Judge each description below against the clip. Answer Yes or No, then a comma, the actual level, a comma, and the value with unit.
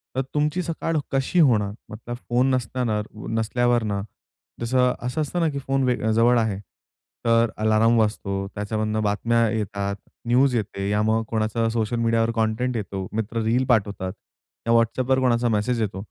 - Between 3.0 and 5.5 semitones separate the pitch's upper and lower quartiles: No, narrow, 2.6 semitones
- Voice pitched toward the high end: No, low, 115 Hz